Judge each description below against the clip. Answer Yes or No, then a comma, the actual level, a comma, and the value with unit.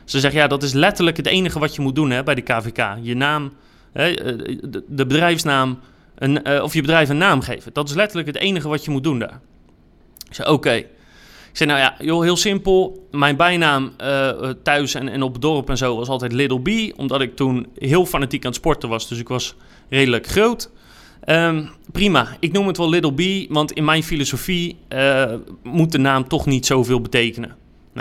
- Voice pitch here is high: No, medium, 140 Hz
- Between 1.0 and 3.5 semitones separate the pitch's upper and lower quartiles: No, average, 3.9 semitones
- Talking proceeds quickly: Yes, fast, 210 wpm